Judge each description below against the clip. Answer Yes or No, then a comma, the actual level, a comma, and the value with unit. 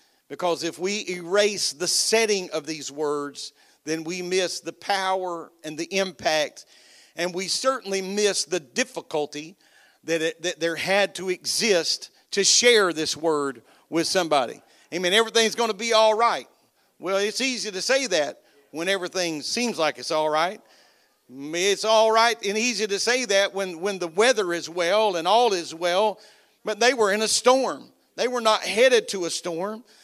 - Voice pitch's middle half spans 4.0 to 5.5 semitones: Yes, average, 4.6 semitones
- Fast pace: No, average, 175 wpm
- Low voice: No, high, 190 Hz